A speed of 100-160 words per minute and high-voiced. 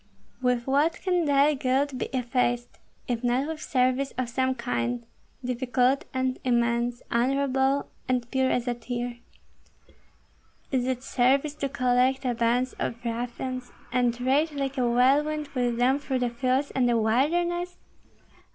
Yes: average, 145 wpm; very high, 255 Hz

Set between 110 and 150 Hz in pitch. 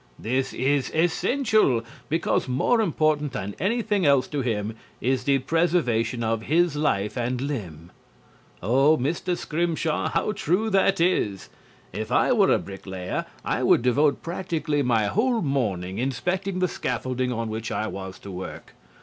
Yes: low, 135 Hz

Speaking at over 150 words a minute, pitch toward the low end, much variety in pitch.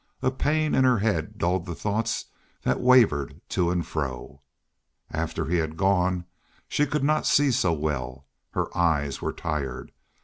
Yes: average, 160 wpm; very low, 85 Hz; wide, 7.2 semitones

